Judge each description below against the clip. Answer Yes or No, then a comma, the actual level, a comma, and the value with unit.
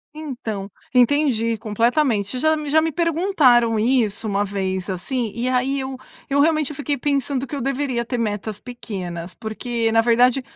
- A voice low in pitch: No, high, 245 Hz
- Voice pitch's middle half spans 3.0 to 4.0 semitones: No, average, 4.4 semitones